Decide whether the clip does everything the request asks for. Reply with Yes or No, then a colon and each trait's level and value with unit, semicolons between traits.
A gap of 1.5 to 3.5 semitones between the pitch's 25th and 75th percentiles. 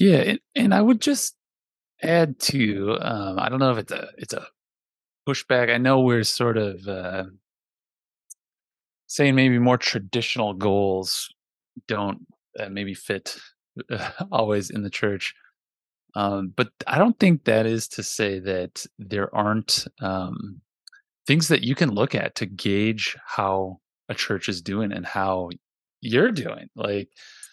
No: average, 5.0 semitones